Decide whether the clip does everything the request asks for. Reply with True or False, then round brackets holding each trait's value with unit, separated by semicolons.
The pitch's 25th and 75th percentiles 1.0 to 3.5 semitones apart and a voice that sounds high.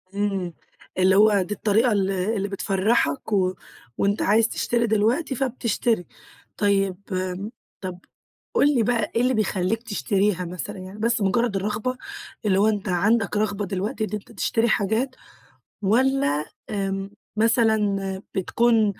True (2.8 semitones; 210 Hz)